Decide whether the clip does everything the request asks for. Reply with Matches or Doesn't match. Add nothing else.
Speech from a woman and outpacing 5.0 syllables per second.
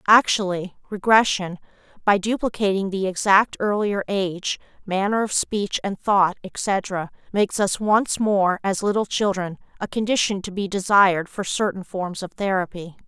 Doesn't match